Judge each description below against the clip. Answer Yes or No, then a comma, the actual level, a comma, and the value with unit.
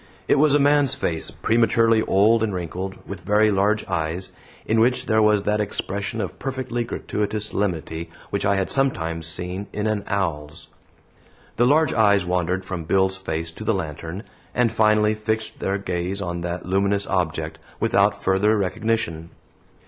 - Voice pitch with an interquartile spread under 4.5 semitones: Yes, average, 3.5 semitones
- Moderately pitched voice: No, low, 100 Hz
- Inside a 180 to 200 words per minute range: No, average, 160 wpm